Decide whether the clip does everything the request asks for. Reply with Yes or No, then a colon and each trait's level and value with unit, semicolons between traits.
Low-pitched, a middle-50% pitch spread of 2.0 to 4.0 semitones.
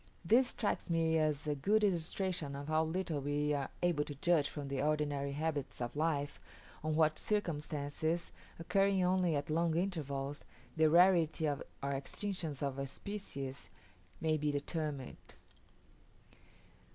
No: medium, 155 Hz; average, 3.2 semitones